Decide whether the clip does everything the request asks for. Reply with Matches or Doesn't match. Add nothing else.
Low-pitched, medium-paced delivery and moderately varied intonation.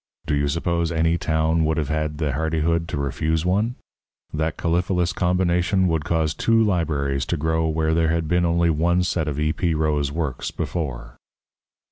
Doesn't match